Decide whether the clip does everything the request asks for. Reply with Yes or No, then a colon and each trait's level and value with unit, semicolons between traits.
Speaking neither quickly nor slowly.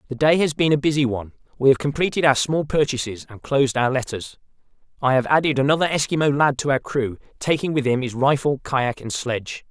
No: fast, 210 wpm